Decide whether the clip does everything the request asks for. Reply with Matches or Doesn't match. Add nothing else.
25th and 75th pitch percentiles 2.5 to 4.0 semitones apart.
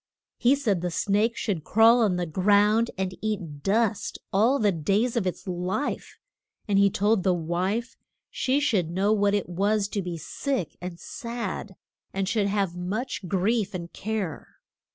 Matches